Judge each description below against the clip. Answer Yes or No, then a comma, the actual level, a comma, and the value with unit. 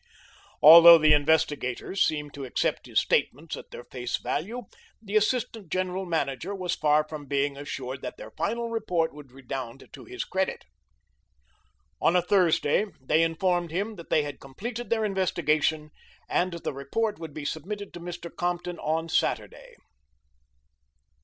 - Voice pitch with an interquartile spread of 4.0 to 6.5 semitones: Yes, average, 4.5 semitones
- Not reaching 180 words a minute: Yes, average, 150 wpm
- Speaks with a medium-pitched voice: Yes, medium, 165 Hz